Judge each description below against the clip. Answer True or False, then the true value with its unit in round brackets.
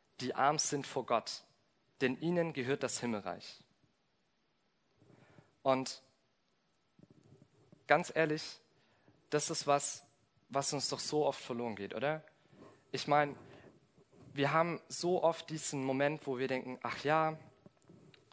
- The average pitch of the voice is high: False (140 Hz)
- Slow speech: True (120 wpm)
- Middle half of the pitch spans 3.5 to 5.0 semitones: False (2.9 semitones)